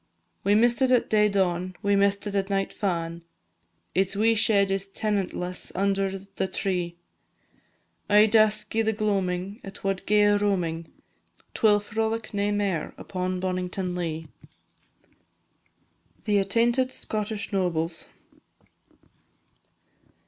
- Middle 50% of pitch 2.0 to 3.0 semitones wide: Yes, narrow, 2.4 semitones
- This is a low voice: No, high, 200 Hz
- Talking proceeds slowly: Yes, slow, 125 wpm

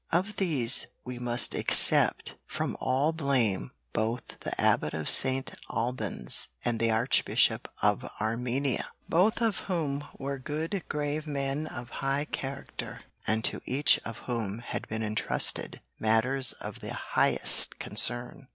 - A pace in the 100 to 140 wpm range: Yes, slow, 135 wpm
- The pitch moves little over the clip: No, average, 4.0 semitones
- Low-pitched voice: Yes, low, 130 Hz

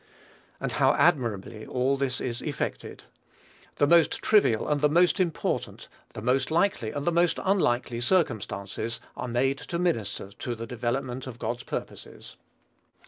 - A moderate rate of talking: Yes, average, 145 wpm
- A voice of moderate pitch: No, low, 130 Hz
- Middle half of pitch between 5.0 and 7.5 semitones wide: Yes, wide, 5.5 semitones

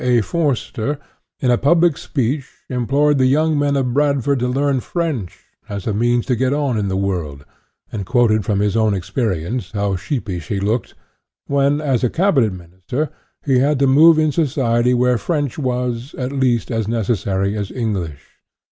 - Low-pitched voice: Yes, low, 125 Hz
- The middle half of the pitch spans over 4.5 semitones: Yes, average, 5.1 semitones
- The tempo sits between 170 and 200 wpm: Yes, average, 175 wpm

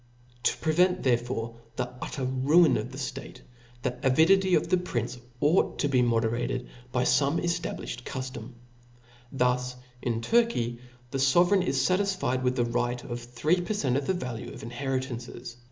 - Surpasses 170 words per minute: No, average, 160 wpm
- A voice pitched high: No, low, 130 Hz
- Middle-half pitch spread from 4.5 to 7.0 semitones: Yes, average, 5.1 semitones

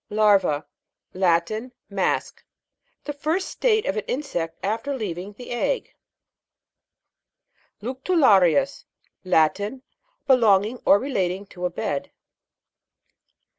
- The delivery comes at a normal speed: No, slow, 100 wpm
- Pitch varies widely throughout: Yes, wide, 6.4 semitones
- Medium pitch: No, high, 210 Hz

